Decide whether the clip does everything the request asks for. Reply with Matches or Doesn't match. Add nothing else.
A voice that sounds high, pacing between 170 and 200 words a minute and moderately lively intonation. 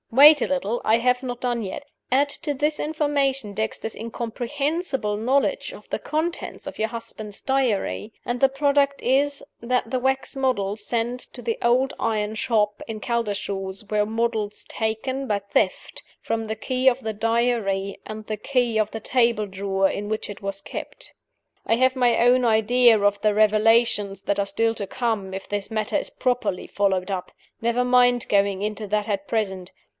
Matches